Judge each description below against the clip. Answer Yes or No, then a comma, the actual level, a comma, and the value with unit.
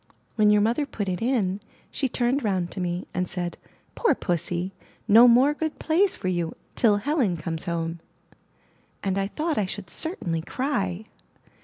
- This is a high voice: Yes, high, 205 Hz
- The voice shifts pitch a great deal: Yes, wide, 6.4 semitones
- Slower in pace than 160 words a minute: No, average, 165 wpm